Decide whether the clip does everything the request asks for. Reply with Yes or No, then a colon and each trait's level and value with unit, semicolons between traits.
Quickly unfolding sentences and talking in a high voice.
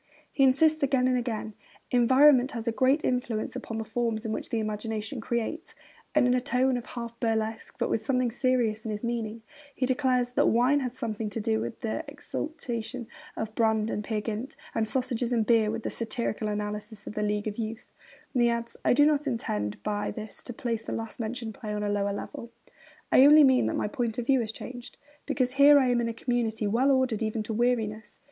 Yes: fast, 215 wpm; high, 235 Hz